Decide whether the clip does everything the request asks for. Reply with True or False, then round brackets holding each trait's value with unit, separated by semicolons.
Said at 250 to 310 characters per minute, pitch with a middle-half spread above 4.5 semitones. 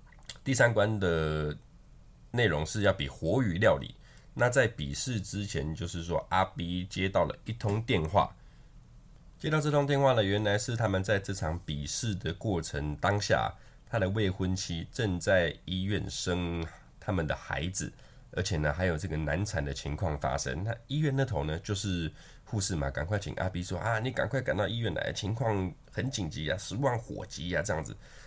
True (260 characters per minute; 5.2 semitones)